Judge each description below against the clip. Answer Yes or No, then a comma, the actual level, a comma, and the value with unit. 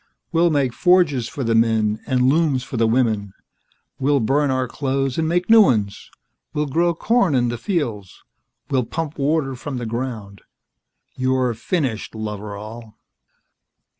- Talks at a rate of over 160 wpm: No, average, 145 wpm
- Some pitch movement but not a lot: Yes, average, 4.8 semitones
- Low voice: Yes, low, 130 Hz